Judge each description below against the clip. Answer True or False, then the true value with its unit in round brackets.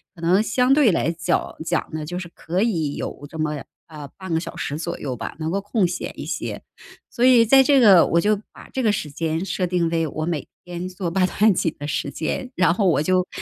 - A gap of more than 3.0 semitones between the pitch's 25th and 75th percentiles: True (4.0 semitones)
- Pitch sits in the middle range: True (175 Hz)